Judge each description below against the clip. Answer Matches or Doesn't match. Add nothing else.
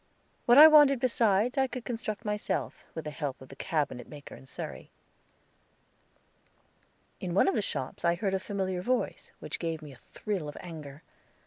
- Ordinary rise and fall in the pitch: Doesn't match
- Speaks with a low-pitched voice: Doesn't match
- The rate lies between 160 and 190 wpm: Matches